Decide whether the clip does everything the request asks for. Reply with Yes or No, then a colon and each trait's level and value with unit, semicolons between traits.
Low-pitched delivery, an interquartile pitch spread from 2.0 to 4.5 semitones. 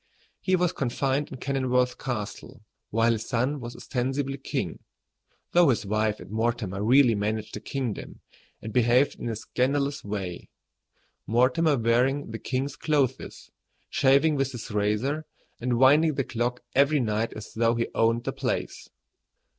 Yes: low, 125 Hz; average, 3.5 semitones